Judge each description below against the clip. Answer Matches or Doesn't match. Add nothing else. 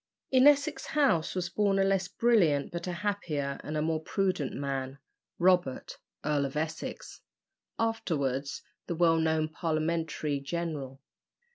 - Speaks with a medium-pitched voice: Matches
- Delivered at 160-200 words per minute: Doesn't match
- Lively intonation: Doesn't match